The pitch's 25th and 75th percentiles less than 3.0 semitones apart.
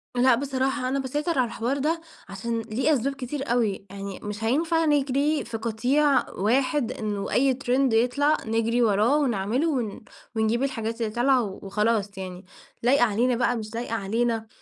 No: average, 3.7 semitones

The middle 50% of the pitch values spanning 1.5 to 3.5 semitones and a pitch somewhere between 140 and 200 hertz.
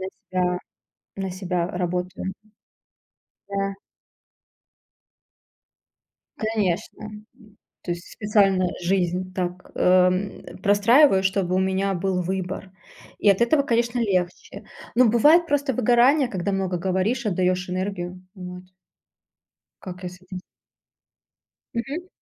Yes: average, 2.9 semitones; high, 190 Hz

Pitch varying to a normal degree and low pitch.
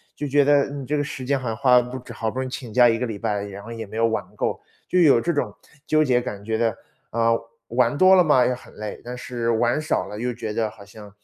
Yes: average, 3.4 semitones; low, 120 Hz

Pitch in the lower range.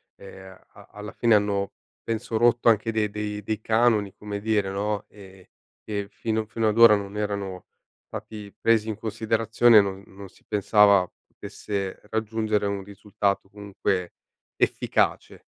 Yes: low, 105 Hz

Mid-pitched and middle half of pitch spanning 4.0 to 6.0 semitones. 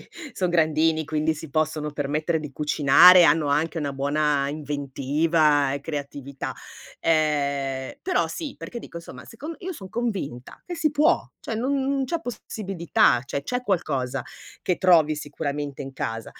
Yes: medium, 155 Hz; average, 4.6 semitones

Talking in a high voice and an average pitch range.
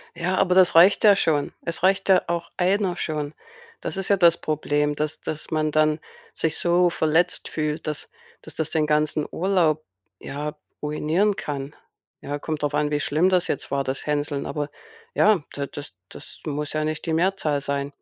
No: medium, 155 Hz; average, 3.0 semitones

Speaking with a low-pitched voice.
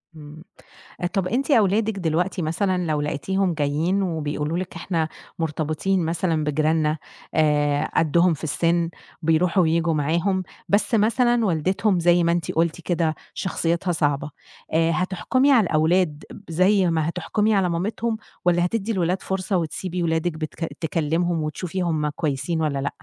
No: medium, 170 Hz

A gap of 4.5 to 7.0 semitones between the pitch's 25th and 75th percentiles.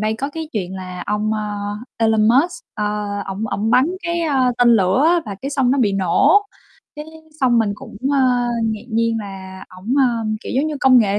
Yes: average, 4.8 semitones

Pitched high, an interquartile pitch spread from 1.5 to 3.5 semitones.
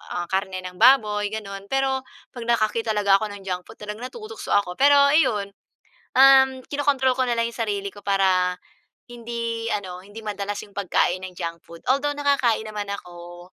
No: high, 210 Hz; average, 4.0 semitones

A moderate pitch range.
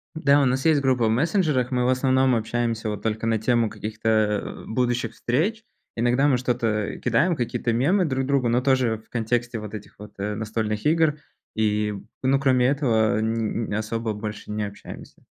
Yes: average, 3.2 semitones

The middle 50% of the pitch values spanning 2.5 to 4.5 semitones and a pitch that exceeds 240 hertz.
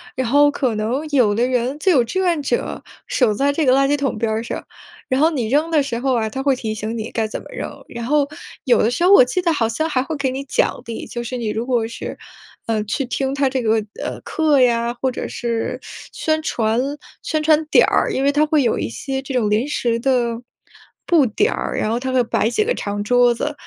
Yes: average, 3.8 semitones; very high, 255 Hz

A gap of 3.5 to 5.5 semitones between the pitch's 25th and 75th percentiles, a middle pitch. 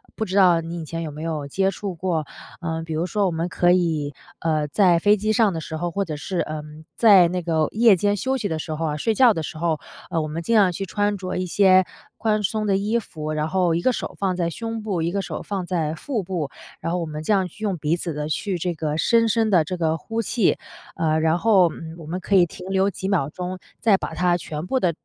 Yes: average, 3.8 semitones; medium, 175 Hz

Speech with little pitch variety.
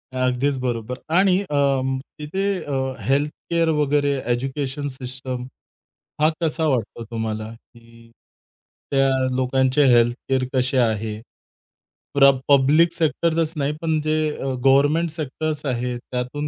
No: average, 3.1 semitones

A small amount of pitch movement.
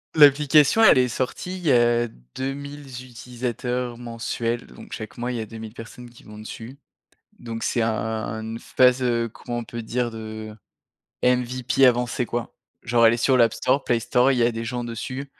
Yes: narrow, 1.8 semitones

